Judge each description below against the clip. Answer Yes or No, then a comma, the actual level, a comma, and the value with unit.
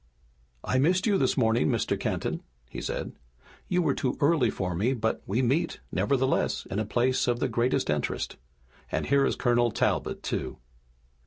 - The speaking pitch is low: Yes, low, 125 Hz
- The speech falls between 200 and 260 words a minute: No, average, 170 wpm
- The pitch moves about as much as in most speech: Yes, average, 3.6 semitones